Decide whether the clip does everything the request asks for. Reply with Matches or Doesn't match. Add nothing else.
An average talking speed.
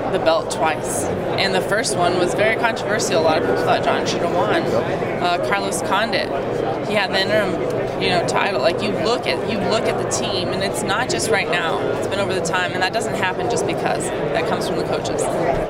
Doesn't match